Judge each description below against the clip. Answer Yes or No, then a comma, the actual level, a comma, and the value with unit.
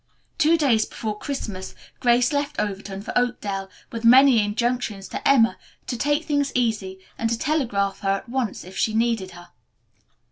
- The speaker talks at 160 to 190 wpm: Yes, average, 165 wpm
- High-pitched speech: Yes, high, 230 Hz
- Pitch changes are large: No, average, 4.8 semitones